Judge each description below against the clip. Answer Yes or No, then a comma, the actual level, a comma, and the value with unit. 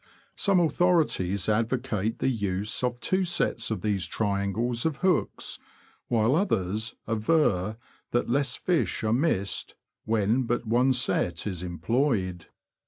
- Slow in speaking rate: Yes, slow, 130 wpm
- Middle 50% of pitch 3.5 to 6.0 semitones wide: Yes, average, 5.1 semitones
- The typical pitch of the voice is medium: No, low, 115 Hz